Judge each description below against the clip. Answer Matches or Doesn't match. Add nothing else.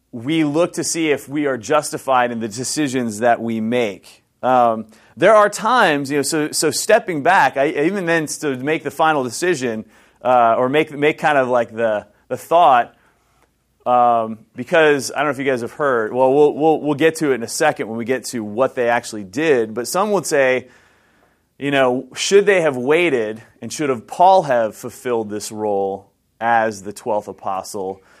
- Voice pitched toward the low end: Matches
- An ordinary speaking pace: Matches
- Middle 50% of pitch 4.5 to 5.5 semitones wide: Matches